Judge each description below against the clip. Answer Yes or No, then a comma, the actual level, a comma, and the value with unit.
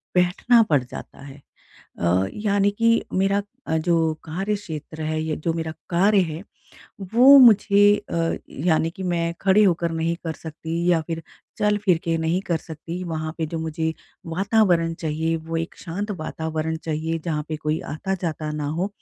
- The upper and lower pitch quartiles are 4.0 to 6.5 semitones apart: No, average, 3.3 semitones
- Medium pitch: Yes, medium, 165 Hz